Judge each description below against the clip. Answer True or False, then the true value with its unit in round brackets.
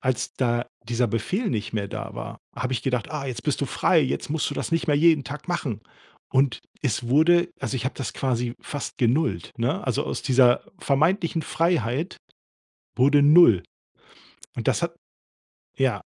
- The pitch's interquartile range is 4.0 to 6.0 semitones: True (4.5 semitones)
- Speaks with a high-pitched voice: False (135 Hz)